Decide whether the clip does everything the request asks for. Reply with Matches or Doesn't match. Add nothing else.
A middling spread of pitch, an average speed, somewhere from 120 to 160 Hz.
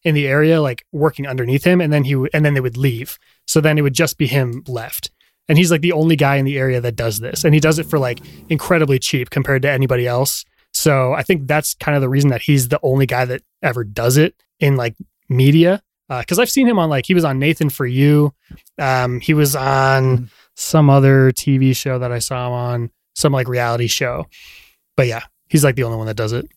Doesn't match